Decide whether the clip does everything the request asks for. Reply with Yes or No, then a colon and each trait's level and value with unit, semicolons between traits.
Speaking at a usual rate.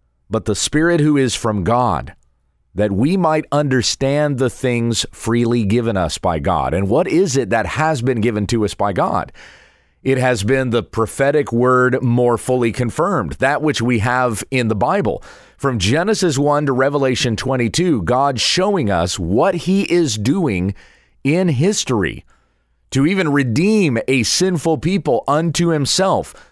Yes: average, 155 wpm